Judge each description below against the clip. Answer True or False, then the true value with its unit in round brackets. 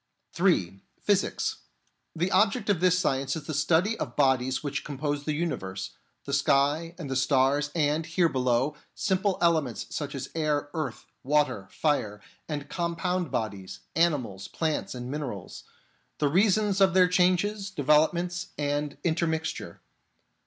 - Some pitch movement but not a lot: True (4.1 semitones)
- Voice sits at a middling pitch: True (150 Hz)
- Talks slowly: False (145 wpm)